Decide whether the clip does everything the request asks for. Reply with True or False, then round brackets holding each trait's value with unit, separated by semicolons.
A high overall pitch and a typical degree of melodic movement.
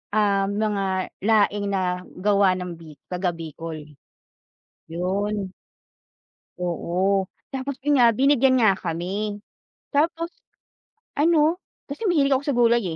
False (200 Hz; 6.2 semitones)